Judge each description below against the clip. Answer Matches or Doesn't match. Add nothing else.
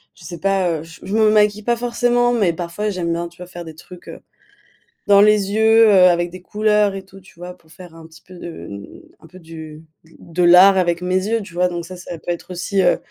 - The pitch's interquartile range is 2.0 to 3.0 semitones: Doesn't match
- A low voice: Doesn't match